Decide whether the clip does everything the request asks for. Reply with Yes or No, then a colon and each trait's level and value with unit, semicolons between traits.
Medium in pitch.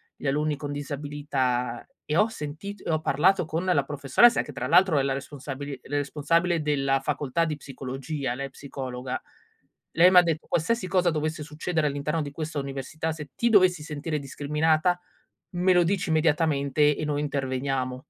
Yes: medium, 150 Hz